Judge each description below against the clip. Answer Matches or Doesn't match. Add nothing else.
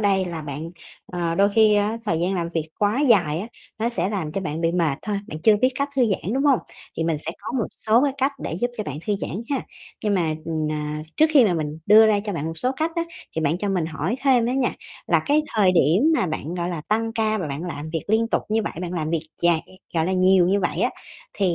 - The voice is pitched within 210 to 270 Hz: Doesn't match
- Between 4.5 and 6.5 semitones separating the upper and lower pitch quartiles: Matches